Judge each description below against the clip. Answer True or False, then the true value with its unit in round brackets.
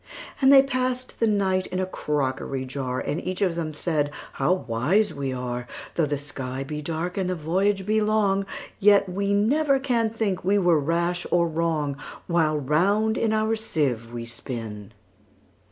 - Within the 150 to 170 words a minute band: True (155 wpm)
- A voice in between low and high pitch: True (175 Hz)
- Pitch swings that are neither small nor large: False (6.2 semitones)